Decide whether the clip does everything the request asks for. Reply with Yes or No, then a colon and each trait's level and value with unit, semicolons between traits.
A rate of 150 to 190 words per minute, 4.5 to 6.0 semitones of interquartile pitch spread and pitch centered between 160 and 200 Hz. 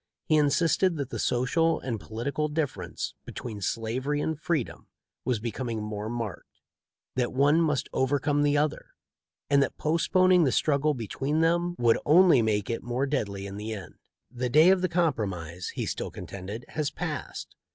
No: average, 165 wpm; wide, 5.4 semitones; low, 135 Hz